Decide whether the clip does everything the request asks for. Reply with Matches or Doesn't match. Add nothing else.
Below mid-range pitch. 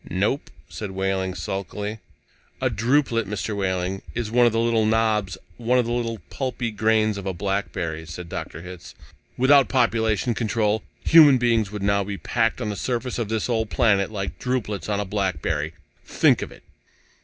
Matches